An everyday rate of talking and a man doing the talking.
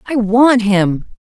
No: average, 145 wpm; female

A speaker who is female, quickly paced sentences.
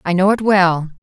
Yes: female; fast, 235 wpm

